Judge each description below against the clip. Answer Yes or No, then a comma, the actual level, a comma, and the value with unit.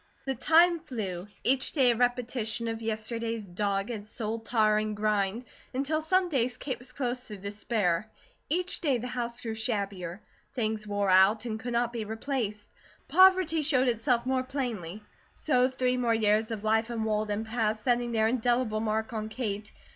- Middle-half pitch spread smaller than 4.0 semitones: Yes, average, 3.0 semitones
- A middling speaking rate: Yes, average, 165 wpm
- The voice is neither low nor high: No, high, 230 Hz